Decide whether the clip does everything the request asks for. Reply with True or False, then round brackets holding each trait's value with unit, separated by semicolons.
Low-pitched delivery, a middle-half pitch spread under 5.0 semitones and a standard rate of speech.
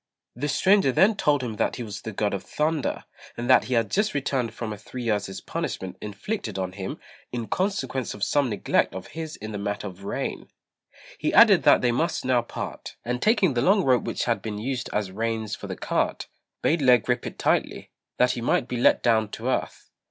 False (120 Hz; 4.5 semitones; 215 wpm)